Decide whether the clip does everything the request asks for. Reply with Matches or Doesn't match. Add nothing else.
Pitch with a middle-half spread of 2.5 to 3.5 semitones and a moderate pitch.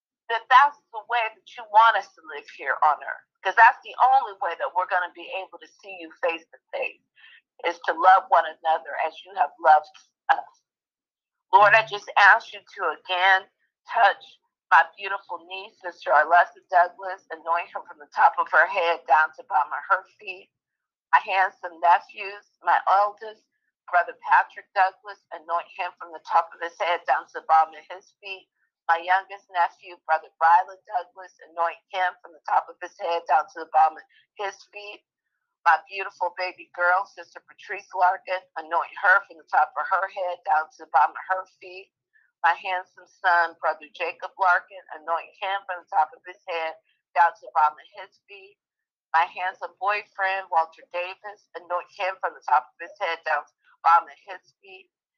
Matches